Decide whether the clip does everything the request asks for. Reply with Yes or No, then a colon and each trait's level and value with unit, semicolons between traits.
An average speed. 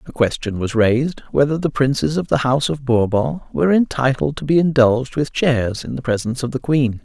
No: fast, 215 wpm